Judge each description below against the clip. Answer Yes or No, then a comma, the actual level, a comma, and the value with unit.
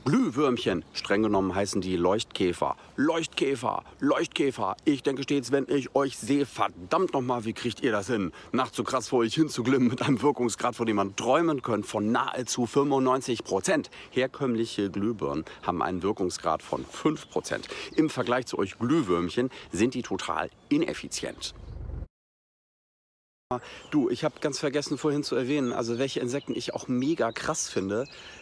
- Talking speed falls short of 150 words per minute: No, average, 155 wpm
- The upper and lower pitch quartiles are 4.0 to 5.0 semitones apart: No, average, 3.5 semitones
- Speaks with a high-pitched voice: No, low, 125 Hz